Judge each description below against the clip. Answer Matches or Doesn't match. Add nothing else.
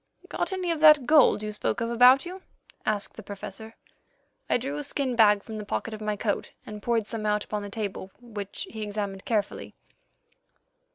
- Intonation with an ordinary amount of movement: Matches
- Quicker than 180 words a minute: Matches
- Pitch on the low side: Doesn't match